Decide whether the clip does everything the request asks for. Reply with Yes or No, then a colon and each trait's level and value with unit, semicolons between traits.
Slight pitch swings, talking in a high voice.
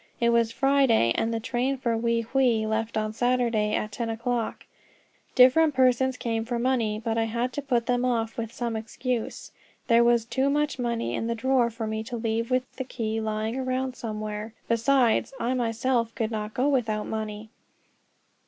Yes: narrow, 2.2 semitones; high, 235 Hz